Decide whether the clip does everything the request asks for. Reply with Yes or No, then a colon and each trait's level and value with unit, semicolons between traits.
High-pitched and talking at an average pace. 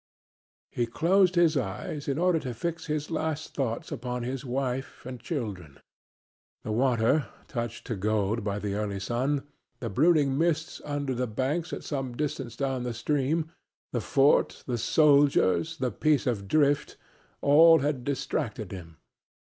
No: low, 135 Hz; average, 150 wpm